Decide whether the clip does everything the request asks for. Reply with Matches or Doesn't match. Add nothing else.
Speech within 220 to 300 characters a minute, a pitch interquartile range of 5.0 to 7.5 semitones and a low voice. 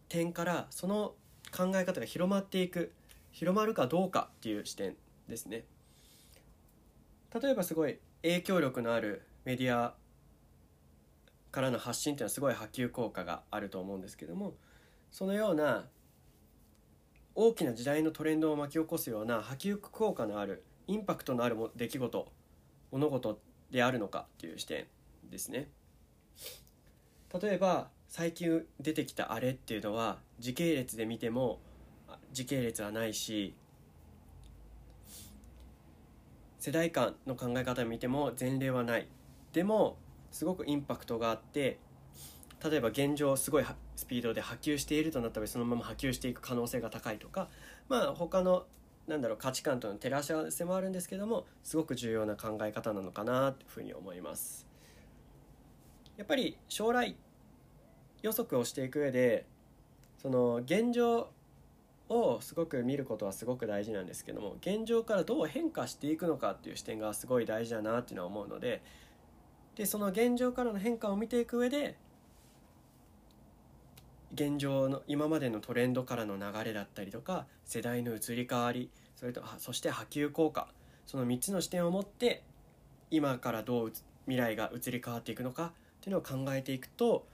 Doesn't match